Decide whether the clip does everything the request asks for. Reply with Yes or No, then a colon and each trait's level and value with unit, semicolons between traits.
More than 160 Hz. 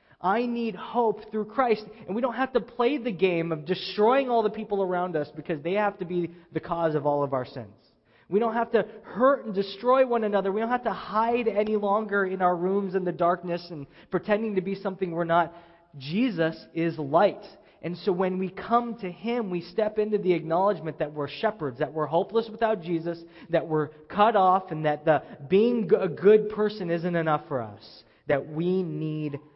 Yes: medium, 185 Hz